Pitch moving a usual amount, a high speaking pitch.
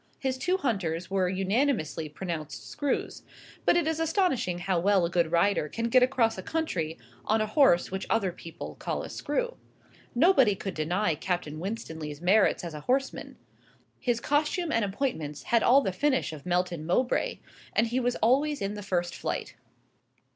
No: wide, 7.0 semitones; high, 200 Hz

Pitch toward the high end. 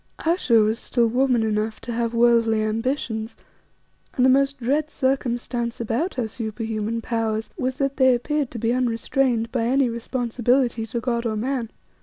Yes: high, 235 Hz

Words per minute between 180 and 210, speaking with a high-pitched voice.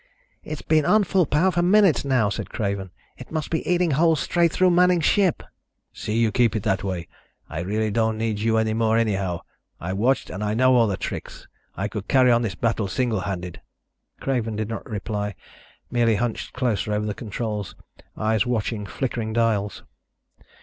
No: average, 185 wpm; low, 115 Hz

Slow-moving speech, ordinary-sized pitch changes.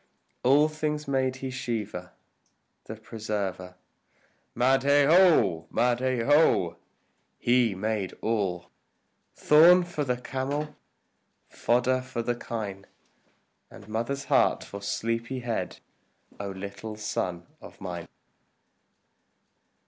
Yes: slow, 95 wpm; average, 4.8 semitones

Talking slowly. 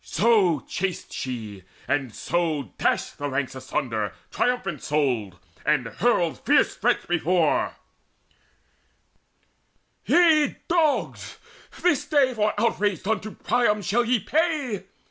Yes: slow, 115 wpm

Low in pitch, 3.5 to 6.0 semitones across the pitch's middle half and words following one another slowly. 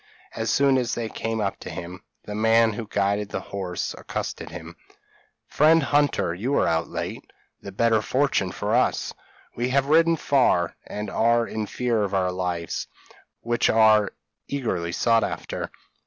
No: low, 110 Hz; average, 4.1 semitones; average, 160 wpm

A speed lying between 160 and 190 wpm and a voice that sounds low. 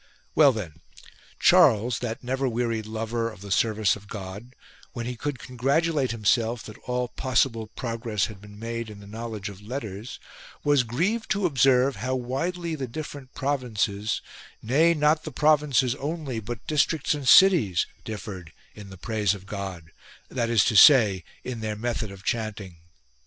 Yes: average, 170 wpm; low, 115 Hz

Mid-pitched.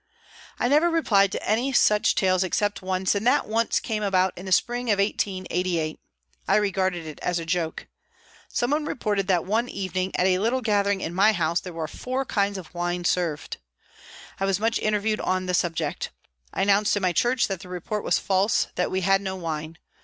No: high, 195 Hz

